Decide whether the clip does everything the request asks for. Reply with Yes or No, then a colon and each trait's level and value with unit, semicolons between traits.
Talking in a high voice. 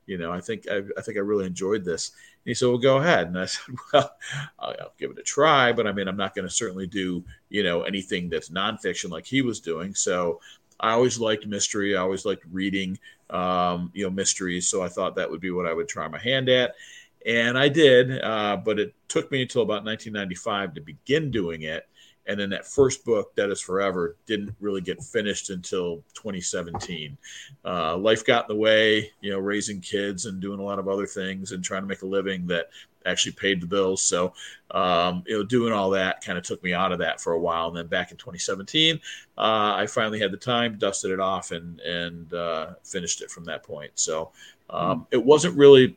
No: low, 100 Hz